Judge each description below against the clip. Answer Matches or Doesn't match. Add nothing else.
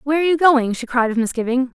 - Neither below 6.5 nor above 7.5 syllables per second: Matches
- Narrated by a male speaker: Doesn't match